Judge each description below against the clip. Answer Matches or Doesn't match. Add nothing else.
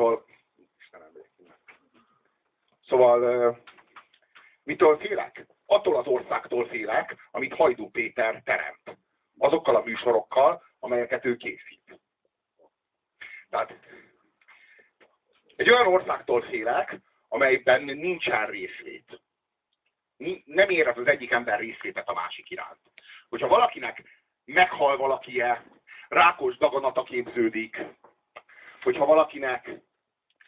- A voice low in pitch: Doesn't match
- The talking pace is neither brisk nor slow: Doesn't match